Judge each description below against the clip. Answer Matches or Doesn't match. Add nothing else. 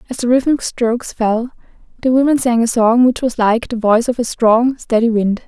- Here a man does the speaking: Doesn't match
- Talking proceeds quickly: Matches